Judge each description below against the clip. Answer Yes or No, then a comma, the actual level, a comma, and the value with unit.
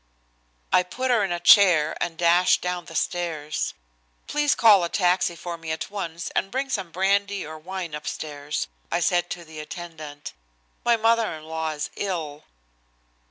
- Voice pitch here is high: No, medium, 175 Hz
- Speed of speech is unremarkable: Yes, average, 165 wpm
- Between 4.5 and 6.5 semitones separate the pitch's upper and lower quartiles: No, average, 3.6 semitones